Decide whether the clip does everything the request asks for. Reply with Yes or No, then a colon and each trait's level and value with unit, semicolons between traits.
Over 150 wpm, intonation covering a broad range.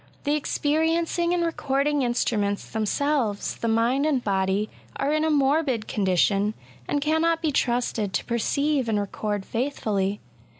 No: average, 140 wpm; wide, 6.2 semitones